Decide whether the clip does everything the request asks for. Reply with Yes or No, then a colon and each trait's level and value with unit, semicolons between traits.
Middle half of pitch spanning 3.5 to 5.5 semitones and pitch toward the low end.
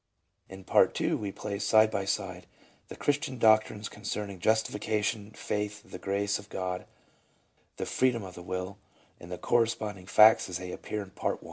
No: narrow, 2.5 semitones; low, 100 Hz